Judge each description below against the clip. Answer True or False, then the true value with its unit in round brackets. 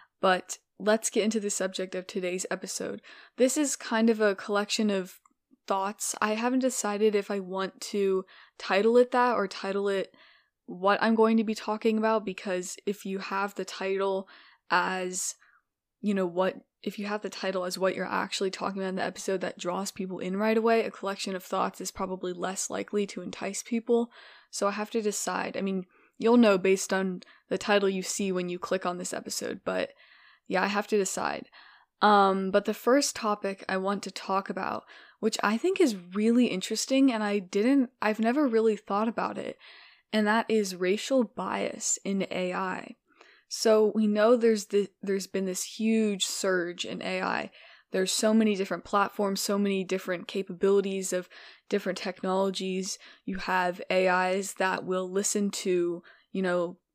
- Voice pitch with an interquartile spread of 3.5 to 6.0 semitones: False (2.6 semitones)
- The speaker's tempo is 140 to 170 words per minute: False (180 wpm)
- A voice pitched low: False (200 Hz)